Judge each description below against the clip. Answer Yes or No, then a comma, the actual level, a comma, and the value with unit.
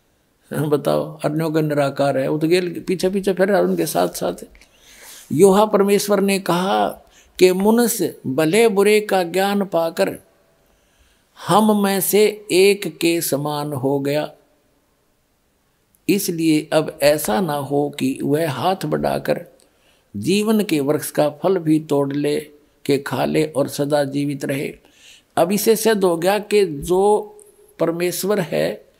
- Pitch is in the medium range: Yes, medium, 170 Hz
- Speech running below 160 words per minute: Yes, average, 135 wpm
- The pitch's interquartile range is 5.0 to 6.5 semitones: Yes, wide, 5.4 semitones